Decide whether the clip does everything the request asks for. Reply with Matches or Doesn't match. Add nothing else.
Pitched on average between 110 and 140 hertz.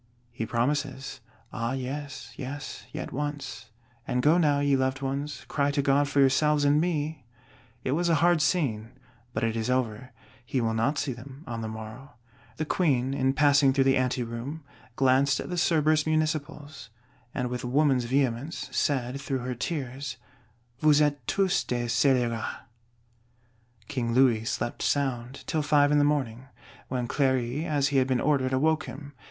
Matches